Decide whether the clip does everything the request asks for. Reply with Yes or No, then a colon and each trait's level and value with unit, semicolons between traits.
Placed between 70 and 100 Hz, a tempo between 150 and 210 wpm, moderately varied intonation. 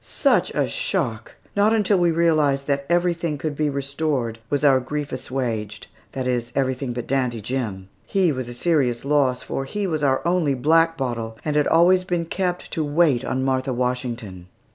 No: medium, 140 Hz; average, 180 wpm; average, 4.6 semitones